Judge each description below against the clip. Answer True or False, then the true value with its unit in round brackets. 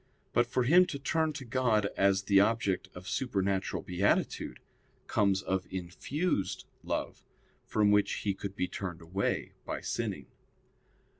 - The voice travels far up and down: False (4.1 semitones)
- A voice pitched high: False (100 Hz)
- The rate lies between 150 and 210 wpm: False (140 wpm)